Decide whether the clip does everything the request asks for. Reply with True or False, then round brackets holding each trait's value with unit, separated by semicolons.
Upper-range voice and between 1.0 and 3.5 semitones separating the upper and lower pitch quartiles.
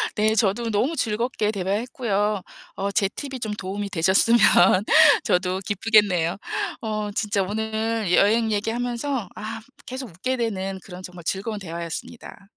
True (210 Hz; 2.9 semitones)